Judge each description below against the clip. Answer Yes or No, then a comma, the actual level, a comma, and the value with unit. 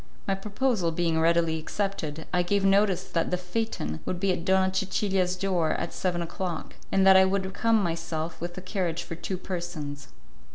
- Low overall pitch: No, medium, 180 Hz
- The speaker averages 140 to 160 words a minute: No, average, 180 wpm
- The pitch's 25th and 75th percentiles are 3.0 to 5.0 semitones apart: No, narrow, 2.5 semitones